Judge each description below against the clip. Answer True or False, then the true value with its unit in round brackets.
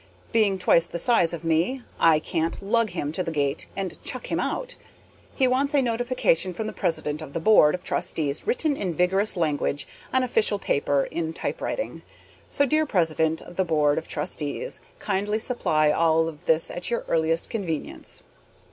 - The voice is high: False (175 Hz)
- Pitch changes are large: True (5.8 semitones)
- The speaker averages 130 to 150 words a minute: False (175 wpm)